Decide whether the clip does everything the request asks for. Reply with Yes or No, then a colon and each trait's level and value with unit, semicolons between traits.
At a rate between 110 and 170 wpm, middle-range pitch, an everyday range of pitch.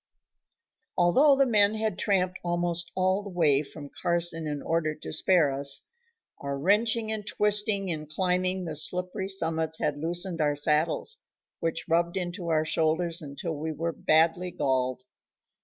Yes: average, 150 wpm; medium, 170 Hz; average, 3.3 semitones